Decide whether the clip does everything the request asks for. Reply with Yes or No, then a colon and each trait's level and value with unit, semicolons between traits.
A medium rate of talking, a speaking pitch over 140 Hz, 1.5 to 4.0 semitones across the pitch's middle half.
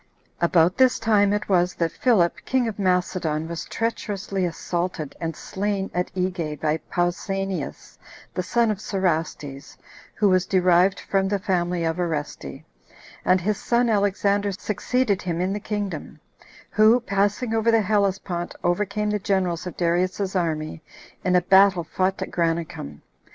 Yes: average, 150 wpm; medium, 185 Hz; average, 2.9 semitones